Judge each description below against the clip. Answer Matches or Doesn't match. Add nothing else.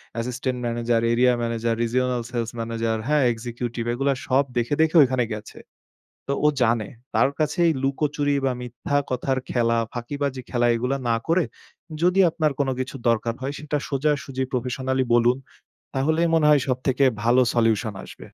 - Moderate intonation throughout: Matches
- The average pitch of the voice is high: Doesn't match